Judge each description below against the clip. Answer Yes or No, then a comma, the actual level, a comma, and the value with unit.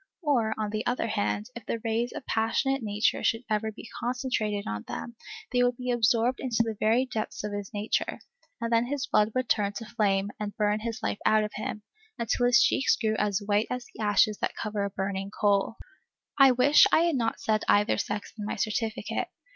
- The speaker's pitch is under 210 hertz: No, high, 220 Hz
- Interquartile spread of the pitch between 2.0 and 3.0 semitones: Yes, narrow, 2.6 semitones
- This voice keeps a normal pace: No, fast, 210 wpm